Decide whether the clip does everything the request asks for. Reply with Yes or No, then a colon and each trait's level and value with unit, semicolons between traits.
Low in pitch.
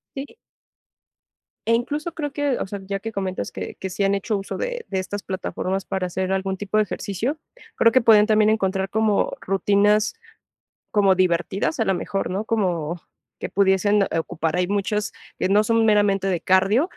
No: high, 200 Hz